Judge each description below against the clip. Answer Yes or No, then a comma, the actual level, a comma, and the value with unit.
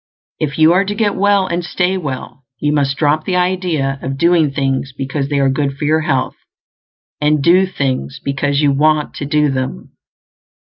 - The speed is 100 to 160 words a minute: No, average, 185 wpm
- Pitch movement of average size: Yes, average, 4.0 semitones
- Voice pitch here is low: No, medium, 150 Hz